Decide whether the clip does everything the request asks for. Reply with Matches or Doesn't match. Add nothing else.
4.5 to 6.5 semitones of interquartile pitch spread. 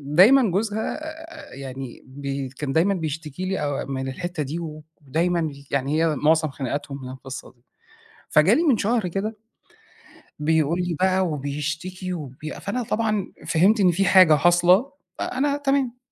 Matches